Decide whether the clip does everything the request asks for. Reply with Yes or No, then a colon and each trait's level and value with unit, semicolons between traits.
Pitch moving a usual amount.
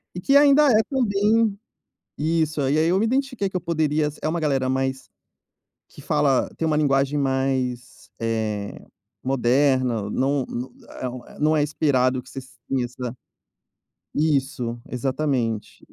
Yes: average, 3.8 semitones